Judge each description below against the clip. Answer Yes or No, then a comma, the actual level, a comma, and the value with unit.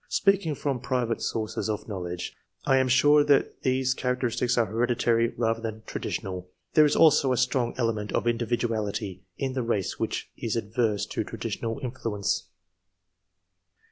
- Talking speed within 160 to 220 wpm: No, average, 150 wpm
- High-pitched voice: No, low, 120 Hz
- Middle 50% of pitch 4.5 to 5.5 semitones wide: No, average, 2.9 semitones